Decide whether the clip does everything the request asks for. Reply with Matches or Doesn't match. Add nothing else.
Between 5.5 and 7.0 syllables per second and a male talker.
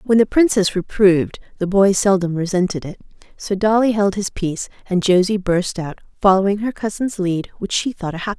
Doesn't match